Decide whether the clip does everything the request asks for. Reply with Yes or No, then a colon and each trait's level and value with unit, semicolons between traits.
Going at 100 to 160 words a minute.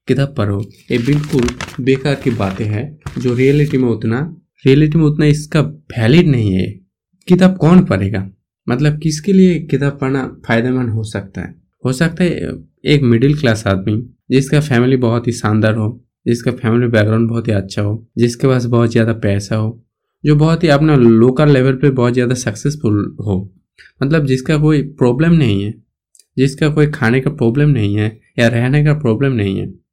No: average, 175 wpm